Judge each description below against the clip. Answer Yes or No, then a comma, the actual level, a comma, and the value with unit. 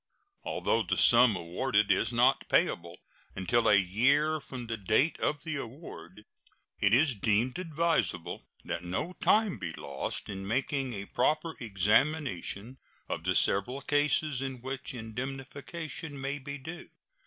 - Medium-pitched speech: No, low, 130 Hz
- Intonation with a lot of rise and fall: Yes, wide, 6.0 semitones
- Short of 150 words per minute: Yes, average, 140 wpm